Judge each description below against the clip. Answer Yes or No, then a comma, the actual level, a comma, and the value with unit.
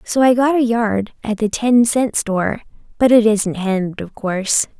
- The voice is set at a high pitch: Yes, high, 220 Hz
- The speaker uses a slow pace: No, average, 190 wpm